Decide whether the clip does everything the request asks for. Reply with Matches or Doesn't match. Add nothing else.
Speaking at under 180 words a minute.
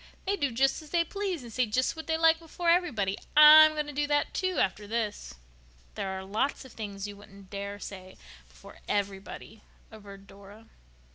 Doesn't match